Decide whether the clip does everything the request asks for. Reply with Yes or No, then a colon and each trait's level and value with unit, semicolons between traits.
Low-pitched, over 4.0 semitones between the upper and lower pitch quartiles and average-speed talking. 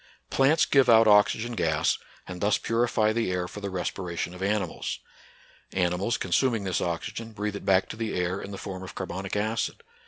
No: low, 100 Hz; average, 3.5 semitones; average, 185 wpm